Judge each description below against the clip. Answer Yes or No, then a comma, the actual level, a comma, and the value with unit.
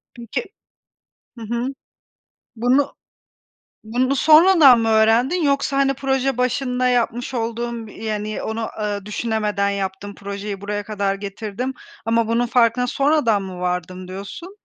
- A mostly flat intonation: No, average, 3.8 semitones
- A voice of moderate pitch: No, high, 230 Hz